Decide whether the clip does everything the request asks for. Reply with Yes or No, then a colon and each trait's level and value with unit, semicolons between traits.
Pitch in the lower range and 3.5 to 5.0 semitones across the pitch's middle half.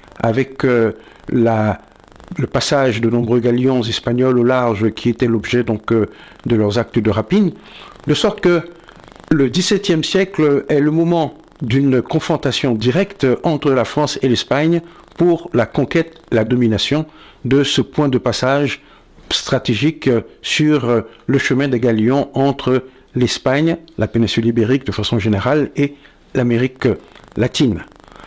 Yes: low, 130 Hz; average, 4.1 semitones